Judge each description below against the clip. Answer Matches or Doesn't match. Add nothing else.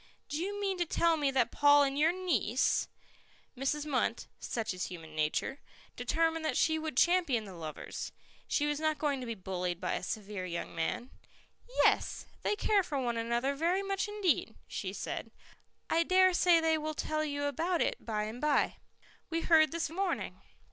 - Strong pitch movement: Matches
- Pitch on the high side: Matches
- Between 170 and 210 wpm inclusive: Matches